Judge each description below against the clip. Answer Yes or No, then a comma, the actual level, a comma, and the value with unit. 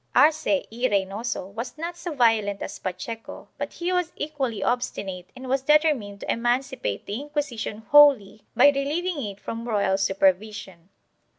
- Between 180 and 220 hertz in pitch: No, high, 240 Hz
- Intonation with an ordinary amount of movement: No, wide, 6.4 semitones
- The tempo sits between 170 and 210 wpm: No, average, 150 wpm